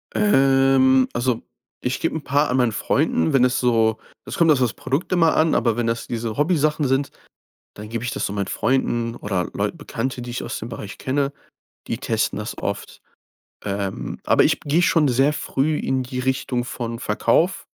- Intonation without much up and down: No, average, 3.2 semitones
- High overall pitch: No, low, 130 Hz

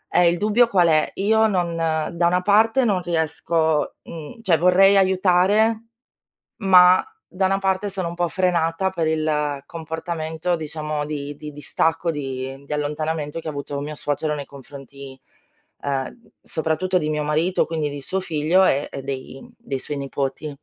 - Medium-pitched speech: Yes, medium, 160 Hz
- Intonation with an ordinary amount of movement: Yes, average, 3.8 semitones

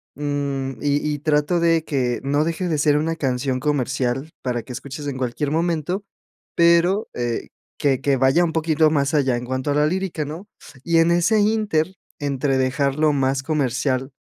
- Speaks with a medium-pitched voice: Yes, medium, 145 Hz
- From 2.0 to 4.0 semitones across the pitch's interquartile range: Yes, average, 3.5 semitones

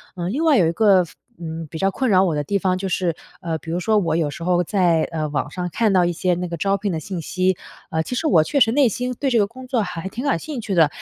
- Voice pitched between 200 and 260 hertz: No, medium, 185 Hz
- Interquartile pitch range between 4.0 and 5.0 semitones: Yes, average, 4.4 semitones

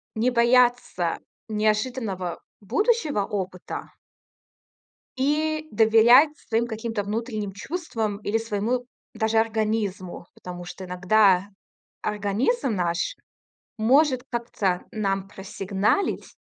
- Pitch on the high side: Yes, high, 220 Hz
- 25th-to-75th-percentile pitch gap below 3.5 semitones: No, average, 3.8 semitones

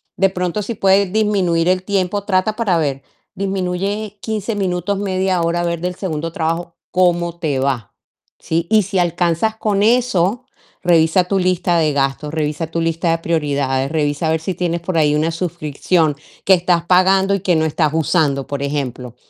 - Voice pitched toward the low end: No, medium, 175 Hz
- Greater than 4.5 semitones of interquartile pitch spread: No, average, 3.1 semitones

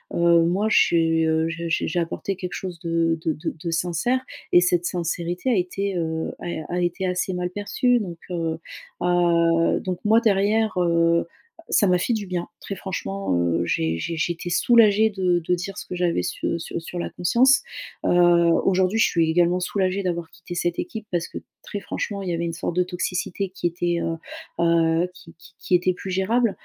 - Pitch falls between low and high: Yes, medium, 175 Hz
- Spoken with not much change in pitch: Yes, narrow, 2.2 semitones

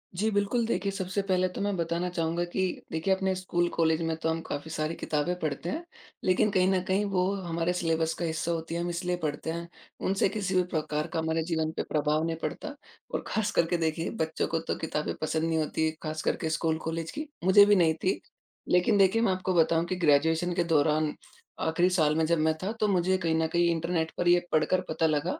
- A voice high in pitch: No, medium, 170 Hz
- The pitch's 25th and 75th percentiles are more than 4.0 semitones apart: No, narrow, 2.4 semitones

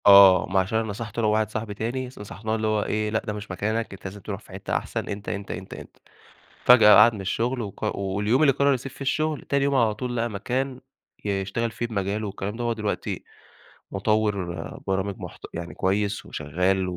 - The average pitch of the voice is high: No, low, 105 Hz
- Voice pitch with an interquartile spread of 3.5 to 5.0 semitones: No, average, 2.9 semitones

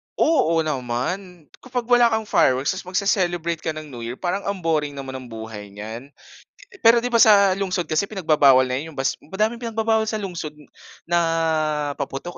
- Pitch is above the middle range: No, medium, 170 Hz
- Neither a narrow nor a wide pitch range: No, wide, 6.9 semitones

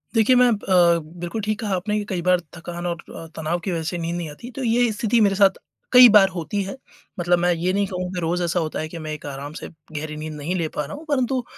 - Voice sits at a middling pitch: Yes, medium, 180 Hz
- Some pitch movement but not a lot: Yes, average, 4.0 semitones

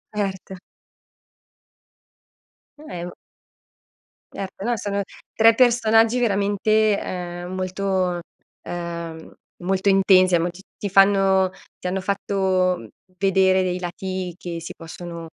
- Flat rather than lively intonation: Yes, narrow, 2.0 semitones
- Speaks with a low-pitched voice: No, high, 190 Hz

